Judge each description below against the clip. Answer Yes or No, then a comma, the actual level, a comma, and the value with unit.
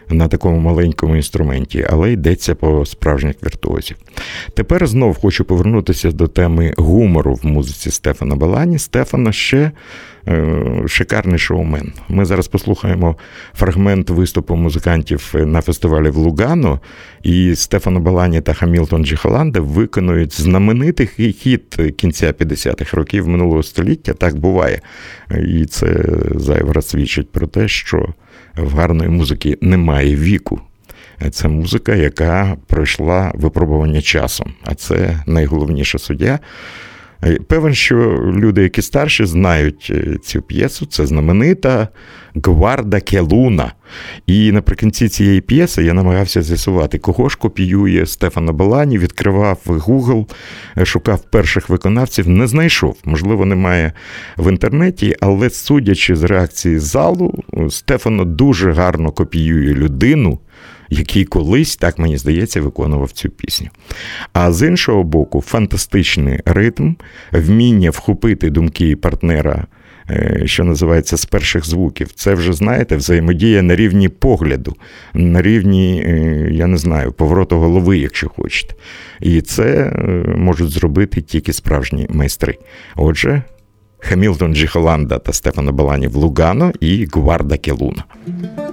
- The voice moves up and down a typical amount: Yes, average, 4.1 semitones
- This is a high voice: No, very low, 90 Hz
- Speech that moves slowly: No, average, 120 wpm